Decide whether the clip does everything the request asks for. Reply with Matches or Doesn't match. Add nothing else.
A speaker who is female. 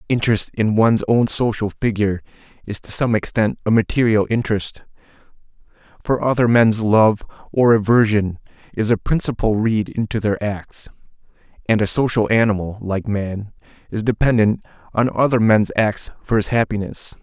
Doesn't match